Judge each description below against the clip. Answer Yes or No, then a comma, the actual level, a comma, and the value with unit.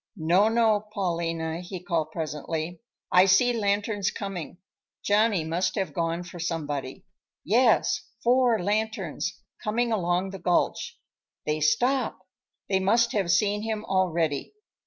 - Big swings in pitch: No, average, 4.3 semitones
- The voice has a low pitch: No, high, 190 Hz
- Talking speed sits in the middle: No, slow, 125 wpm